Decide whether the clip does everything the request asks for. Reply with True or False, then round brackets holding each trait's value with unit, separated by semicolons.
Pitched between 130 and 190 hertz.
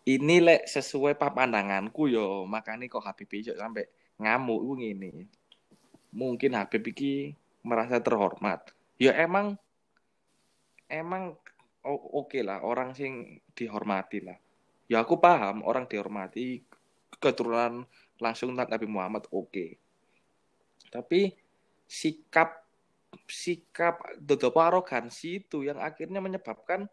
True (135 Hz)